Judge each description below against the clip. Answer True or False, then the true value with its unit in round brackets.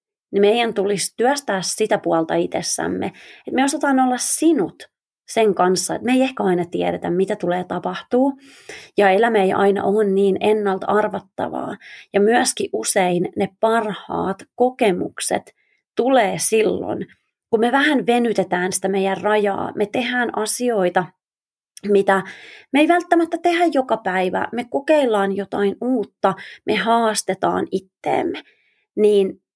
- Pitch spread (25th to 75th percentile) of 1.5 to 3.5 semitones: False (4.5 semitones)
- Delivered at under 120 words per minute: False (130 wpm)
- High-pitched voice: True (210 Hz)